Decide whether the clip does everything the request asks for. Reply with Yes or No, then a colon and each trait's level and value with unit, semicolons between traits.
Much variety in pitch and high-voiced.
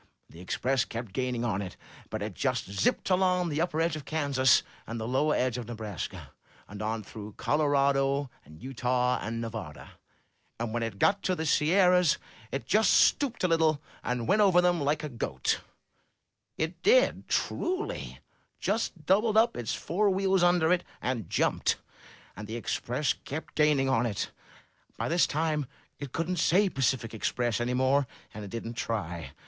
No: wide, 6.7 semitones; low, 135 Hz